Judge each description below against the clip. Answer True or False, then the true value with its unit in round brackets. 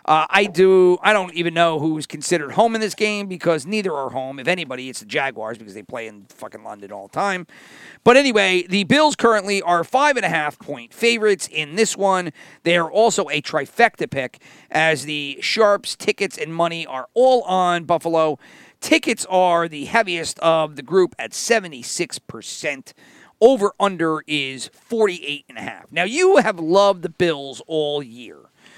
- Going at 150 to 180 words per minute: True (175 wpm)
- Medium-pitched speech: True (175 Hz)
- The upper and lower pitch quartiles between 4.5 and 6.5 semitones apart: True (5.2 semitones)